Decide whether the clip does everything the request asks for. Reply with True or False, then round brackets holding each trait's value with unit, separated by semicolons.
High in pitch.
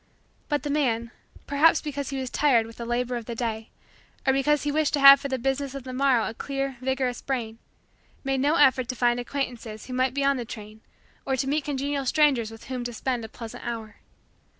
True (260 Hz)